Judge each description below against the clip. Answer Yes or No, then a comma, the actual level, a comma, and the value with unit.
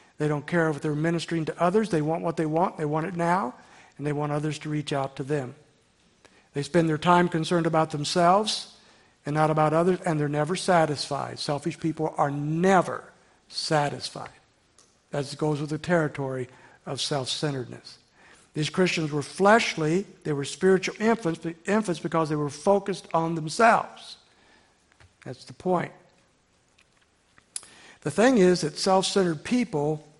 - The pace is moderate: Yes, average, 155 wpm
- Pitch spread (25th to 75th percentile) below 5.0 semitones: Yes, average, 2.9 semitones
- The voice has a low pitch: No, medium, 160 Hz